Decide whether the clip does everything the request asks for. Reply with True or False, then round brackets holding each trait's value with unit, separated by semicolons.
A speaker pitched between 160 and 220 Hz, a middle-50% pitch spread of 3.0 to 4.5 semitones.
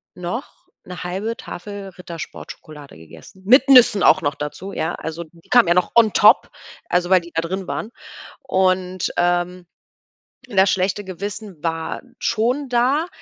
True (185 Hz; 3.5 semitones)